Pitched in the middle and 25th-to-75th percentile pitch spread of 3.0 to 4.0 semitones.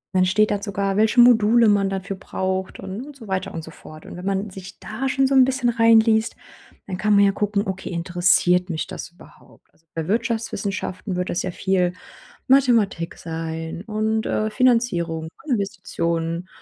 No: high, 195 Hz; average, 3.6 semitones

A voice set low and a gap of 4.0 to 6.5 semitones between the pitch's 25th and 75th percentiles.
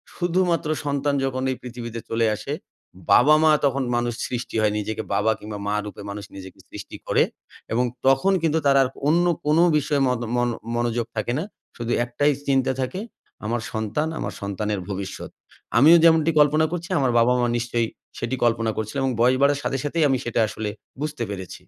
Yes: low, 125 Hz; average, 4.6 semitones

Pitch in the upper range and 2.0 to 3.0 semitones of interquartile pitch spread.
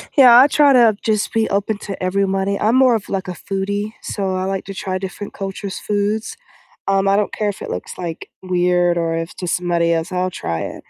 Yes: high, 195 Hz; narrow, 2.5 semitones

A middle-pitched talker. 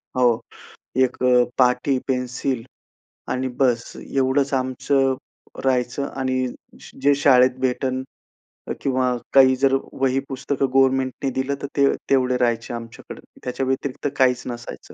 No: low, 130 Hz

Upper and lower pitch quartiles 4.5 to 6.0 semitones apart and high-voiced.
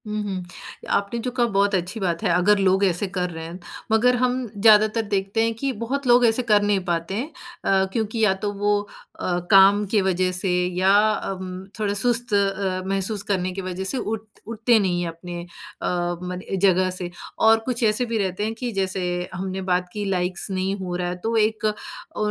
No: average, 3.0 semitones; high, 195 Hz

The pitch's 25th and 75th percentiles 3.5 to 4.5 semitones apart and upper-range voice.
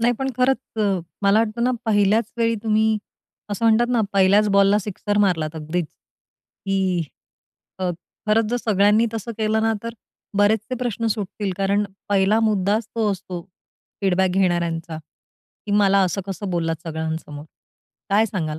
No: average, 3.1 semitones; high, 205 Hz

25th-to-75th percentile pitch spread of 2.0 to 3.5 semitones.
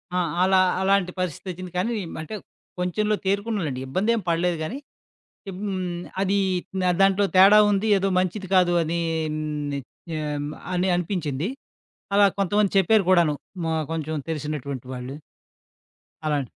No: average, 3.9 semitones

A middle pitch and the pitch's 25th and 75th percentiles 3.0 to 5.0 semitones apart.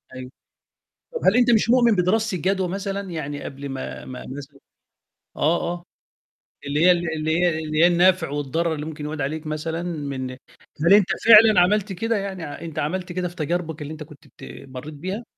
Yes: medium, 170 Hz; average, 4.1 semitones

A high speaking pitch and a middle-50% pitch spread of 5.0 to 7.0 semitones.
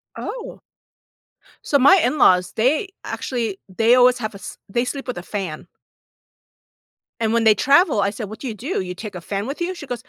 Yes: high, 235 Hz; wide, 5.5 semitones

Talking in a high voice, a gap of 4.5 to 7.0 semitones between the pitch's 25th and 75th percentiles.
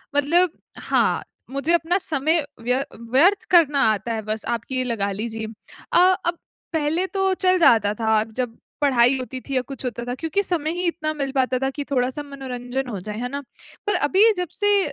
Yes: very high, 275 Hz; wide, 5.6 semitones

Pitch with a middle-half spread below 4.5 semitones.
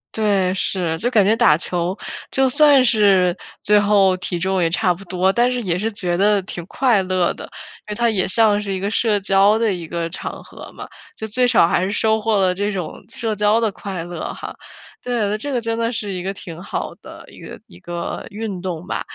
Yes: average, 3.4 semitones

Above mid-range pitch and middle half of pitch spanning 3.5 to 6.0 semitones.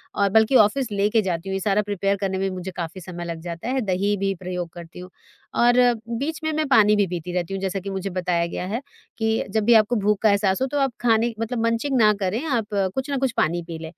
Yes: high, 200 Hz; average, 4.1 semitones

